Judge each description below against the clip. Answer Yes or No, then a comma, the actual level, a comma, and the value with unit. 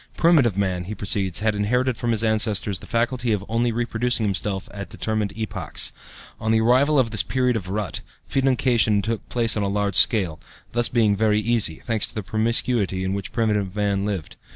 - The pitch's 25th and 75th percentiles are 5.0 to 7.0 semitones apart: No, average, 2.8 semitones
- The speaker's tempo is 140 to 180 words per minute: No, average, 190 wpm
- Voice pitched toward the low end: Yes, low, 110 Hz